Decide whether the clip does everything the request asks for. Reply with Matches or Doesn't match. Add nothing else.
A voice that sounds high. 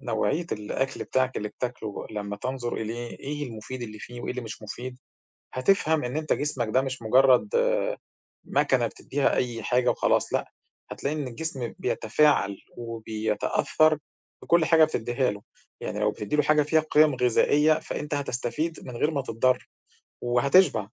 Doesn't match